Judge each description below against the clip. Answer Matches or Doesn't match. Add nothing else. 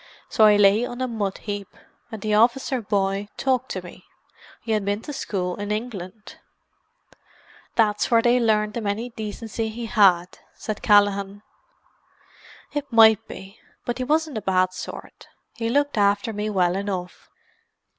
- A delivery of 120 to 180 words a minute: Matches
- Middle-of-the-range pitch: Doesn't match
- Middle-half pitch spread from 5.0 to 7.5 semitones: Doesn't match